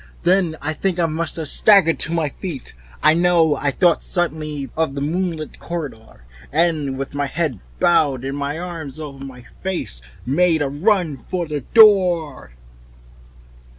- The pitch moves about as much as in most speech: Yes, average, 3.6 semitones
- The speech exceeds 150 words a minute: Yes, average, 160 wpm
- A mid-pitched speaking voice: Yes, medium, 155 Hz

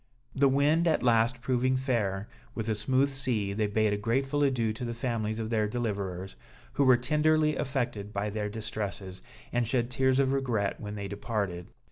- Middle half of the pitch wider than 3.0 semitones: Yes, average, 4.1 semitones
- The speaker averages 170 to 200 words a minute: Yes, average, 180 wpm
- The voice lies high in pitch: No, low, 115 Hz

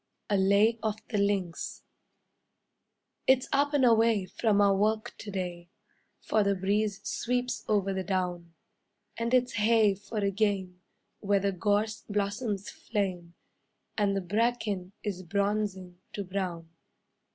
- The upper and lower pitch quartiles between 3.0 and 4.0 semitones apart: No, narrow, 2.5 semitones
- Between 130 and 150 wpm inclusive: Yes, slow, 135 wpm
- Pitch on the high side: Yes, high, 200 Hz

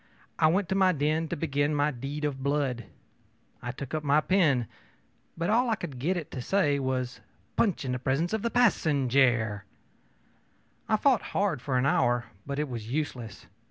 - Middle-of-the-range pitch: Yes, medium, 145 Hz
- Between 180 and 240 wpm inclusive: Yes, average, 185 wpm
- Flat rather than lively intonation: No, average, 4.9 semitones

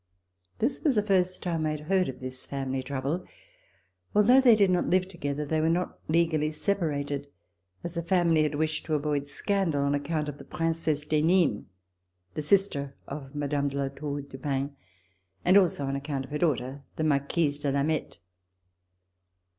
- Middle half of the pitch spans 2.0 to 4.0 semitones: Yes, average, 3.5 semitones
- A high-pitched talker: No, medium, 150 Hz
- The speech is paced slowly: No, average, 180 wpm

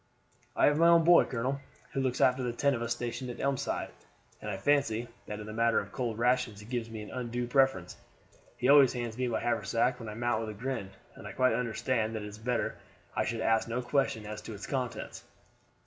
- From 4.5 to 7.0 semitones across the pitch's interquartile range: No, narrow, 2.6 semitones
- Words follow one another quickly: Yes, fast, 230 wpm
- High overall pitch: No, low, 120 Hz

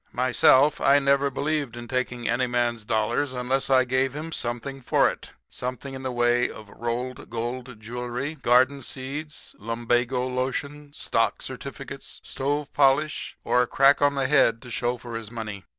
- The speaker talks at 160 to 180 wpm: Yes, average, 165 wpm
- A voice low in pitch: Yes, low, 125 Hz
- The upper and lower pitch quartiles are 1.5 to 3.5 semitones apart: Yes, narrow, 2.4 semitones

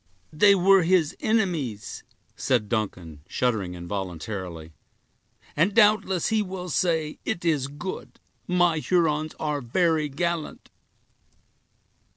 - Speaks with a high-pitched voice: No, medium, 155 Hz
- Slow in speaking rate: Yes, slow, 105 wpm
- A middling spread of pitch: No, wide, 8.3 semitones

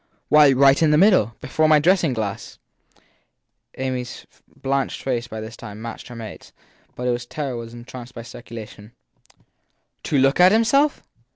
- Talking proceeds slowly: No, average, 165 wpm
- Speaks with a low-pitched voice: Yes, low, 125 Hz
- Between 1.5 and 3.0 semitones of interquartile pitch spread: No, average, 4.3 semitones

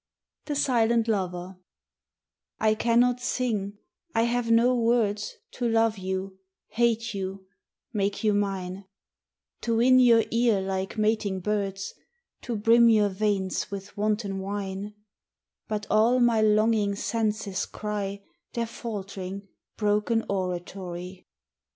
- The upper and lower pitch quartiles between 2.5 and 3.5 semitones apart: Yes, average, 2.8 semitones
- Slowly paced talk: Yes, slow, 120 wpm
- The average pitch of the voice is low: No, high, 210 Hz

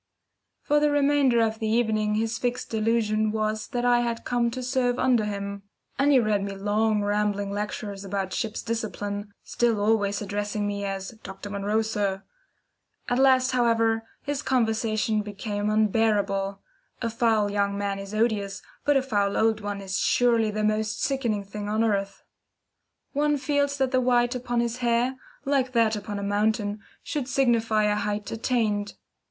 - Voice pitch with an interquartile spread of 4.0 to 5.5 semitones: No, average, 2.9 semitones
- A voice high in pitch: Yes, high, 220 Hz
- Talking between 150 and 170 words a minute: Yes, average, 165 wpm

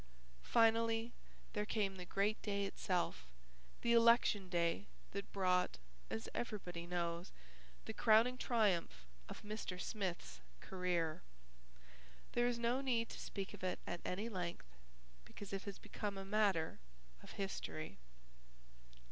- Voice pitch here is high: Yes, high, 195 Hz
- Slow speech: Yes, slow, 130 wpm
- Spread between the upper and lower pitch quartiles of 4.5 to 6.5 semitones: No, average, 4.0 semitones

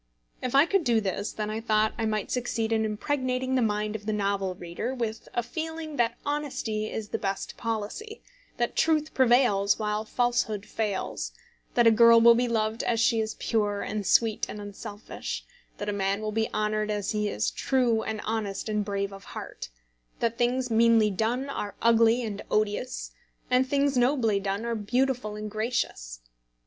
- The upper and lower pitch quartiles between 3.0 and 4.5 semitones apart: No, narrow, 2.6 semitones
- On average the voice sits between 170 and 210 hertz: No, high, 220 Hz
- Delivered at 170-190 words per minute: Yes, average, 180 wpm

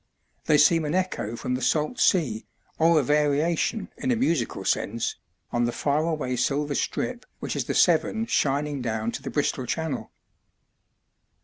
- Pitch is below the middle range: No, medium, 150 Hz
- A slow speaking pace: No, average, 165 wpm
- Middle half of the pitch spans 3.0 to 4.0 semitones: No, average, 4.7 semitones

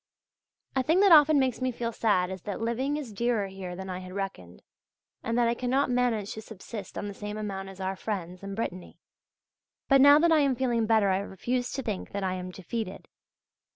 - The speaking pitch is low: No, high, 220 Hz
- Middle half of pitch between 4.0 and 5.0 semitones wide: Yes, average, 4.6 semitones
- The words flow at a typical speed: No, fast, 215 wpm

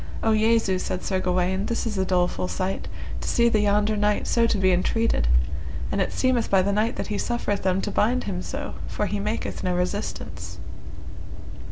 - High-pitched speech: Yes, high, 205 Hz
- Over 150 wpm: Yes, average, 195 wpm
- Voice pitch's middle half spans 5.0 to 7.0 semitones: No, average, 3.2 semitones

